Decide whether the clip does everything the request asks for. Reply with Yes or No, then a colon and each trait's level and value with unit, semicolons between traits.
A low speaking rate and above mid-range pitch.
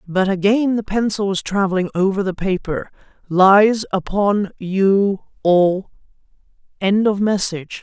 Yes: slow, 115 wpm; high, 195 Hz